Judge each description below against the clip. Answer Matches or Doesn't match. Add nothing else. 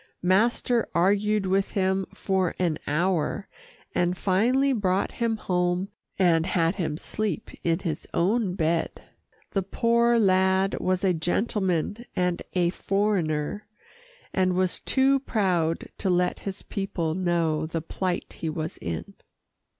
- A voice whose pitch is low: Doesn't match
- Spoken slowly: Matches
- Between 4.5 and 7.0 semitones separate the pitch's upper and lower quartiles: Doesn't match